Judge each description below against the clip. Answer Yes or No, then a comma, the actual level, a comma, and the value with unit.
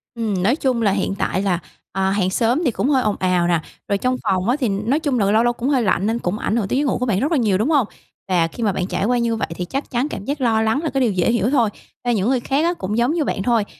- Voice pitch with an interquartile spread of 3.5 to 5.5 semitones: Yes, average, 4.6 semitones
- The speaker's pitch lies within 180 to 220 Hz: No, high, 230 Hz